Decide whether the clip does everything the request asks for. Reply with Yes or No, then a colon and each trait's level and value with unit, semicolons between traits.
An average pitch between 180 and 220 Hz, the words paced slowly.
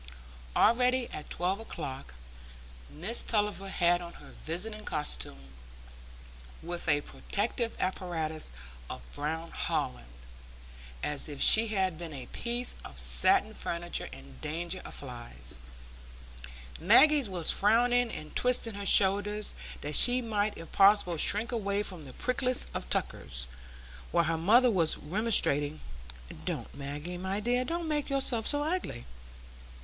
Yes: high, 190 Hz; slow, 130 wpm